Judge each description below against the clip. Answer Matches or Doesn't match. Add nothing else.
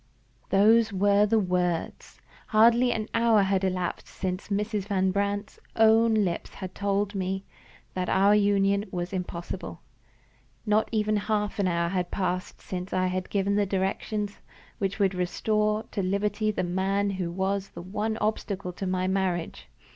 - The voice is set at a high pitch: Matches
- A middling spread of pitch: Doesn't match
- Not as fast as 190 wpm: Matches